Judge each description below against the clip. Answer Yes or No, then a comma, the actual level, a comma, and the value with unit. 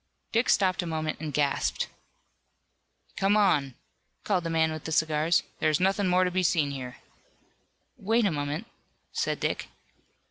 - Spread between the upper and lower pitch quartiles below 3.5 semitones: No, average, 3.8 semitones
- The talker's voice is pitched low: No, medium, 165 Hz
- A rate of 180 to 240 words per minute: No, average, 155 wpm